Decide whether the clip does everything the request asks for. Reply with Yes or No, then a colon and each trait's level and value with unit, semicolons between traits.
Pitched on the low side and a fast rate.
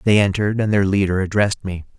Yes: low, 100 Hz; fast, 210 wpm